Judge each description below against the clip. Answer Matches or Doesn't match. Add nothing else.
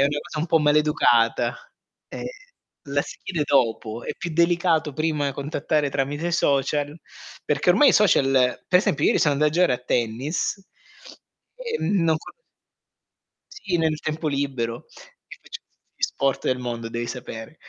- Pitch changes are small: Doesn't match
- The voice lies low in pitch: Doesn't match